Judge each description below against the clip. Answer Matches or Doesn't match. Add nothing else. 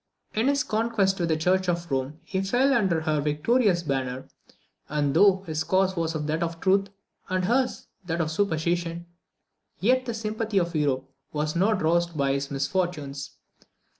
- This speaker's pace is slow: Doesn't match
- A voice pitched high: Doesn't match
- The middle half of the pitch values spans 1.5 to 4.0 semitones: Doesn't match